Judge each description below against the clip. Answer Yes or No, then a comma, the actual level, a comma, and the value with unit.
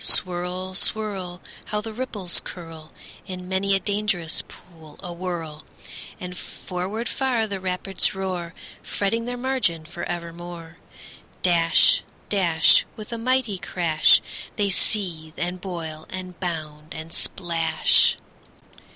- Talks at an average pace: No, slow, 115 wpm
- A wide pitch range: No, average, 3.2 semitones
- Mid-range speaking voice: Yes, medium, 180 Hz